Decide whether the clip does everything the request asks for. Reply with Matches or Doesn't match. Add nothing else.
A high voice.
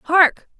Matches